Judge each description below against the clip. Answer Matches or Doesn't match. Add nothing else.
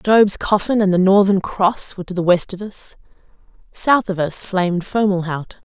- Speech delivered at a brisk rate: Doesn't match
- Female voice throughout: Matches